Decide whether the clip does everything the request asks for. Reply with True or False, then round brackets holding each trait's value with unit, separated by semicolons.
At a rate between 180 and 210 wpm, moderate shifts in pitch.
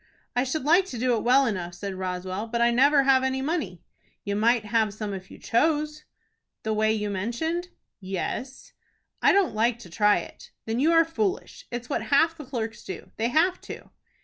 False (200 wpm; 5.9 semitones)